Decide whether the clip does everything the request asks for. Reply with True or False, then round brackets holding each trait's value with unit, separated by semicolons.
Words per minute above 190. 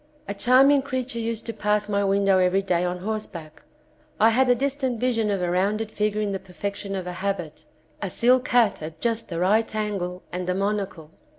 True (200 wpm)